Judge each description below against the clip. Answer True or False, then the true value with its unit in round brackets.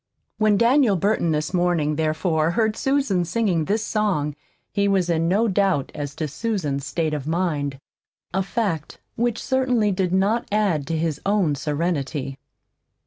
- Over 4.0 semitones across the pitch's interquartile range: True (5.5 semitones)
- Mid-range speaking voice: True (180 Hz)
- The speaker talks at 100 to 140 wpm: False (150 wpm)